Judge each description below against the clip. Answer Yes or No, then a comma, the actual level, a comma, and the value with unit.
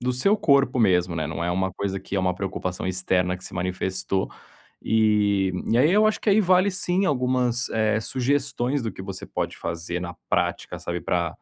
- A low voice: Yes, low, 105 Hz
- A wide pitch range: Yes, wide, 6.4 semitones